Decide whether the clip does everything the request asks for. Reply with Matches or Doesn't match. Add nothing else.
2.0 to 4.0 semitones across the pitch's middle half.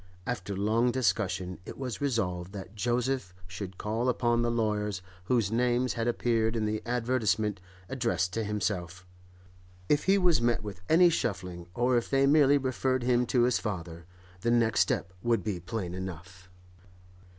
Doesn't match